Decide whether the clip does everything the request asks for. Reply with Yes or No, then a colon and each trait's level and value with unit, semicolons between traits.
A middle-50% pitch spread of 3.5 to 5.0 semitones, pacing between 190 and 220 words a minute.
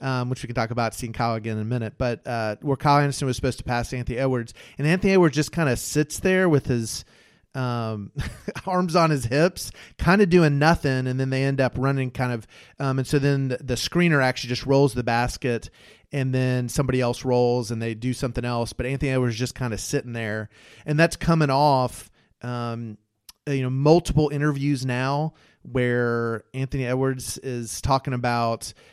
No: average, 3.0 semitones; average, 200 wpm